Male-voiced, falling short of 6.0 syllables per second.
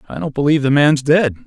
No: male; 6.6 syllables/s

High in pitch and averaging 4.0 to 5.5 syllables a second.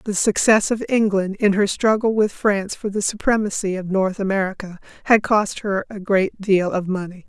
Yes: high, 200 Hz; 5.0 syllables/s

